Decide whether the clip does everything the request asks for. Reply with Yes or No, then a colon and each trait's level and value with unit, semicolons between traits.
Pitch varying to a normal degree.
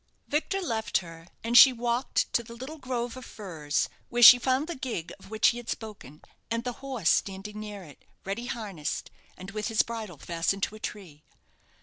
Yes: average, 4.1 semitones